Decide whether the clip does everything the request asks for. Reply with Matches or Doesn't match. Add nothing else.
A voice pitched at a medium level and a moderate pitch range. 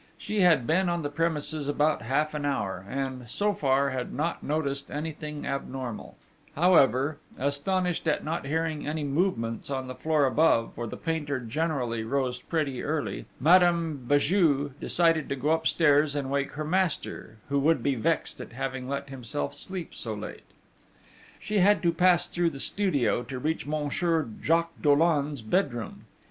Matches